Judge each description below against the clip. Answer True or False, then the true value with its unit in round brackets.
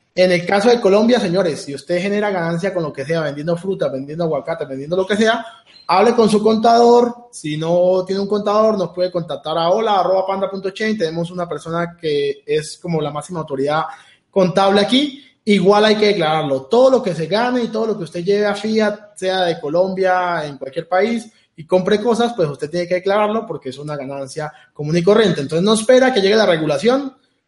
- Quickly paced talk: True (200 wpm)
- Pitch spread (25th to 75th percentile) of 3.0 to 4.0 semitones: False (4.9 semitones)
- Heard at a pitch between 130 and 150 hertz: False (190 Hz)